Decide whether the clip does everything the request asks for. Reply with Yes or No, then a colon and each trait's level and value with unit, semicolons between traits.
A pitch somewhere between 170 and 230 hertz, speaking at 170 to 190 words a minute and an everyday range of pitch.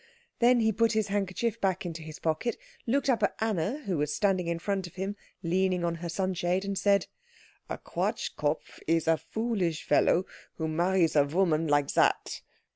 Yes: medium, 185 Hz; average, 180 wpm; average, 3.7 semitones